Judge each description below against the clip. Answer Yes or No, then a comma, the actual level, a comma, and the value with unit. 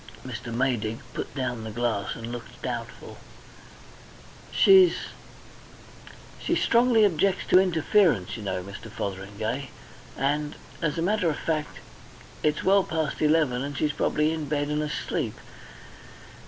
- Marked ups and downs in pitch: Yes, wide, 5.9 semitones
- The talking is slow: Yes, slow, 130 wpm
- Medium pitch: Yes, medium, 145 Hz